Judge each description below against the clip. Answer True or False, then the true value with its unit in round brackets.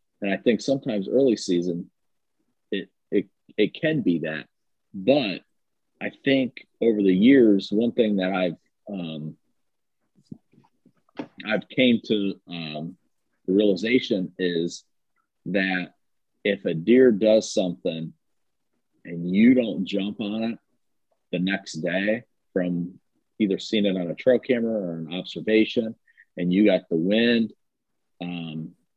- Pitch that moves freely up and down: False (4.1 semitones)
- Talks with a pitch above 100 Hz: False (95 Hz)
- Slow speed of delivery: True (130 wpm)